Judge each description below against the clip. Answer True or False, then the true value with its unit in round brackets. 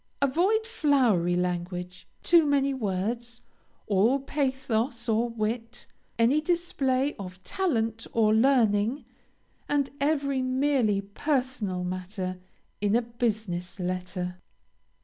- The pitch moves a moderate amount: False (5.9 semitones)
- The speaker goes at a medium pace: False (100 wpm)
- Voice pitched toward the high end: True (230 Hz)